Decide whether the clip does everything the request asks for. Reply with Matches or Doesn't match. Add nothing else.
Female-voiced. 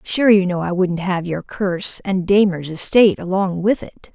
Matches